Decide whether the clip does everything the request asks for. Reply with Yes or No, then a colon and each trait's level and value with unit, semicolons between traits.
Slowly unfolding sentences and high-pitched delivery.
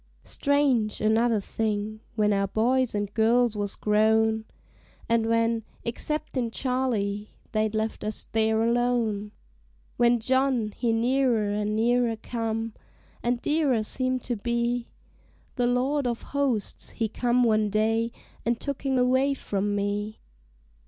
Yes: slow, 130 wpm; high, 230 Hz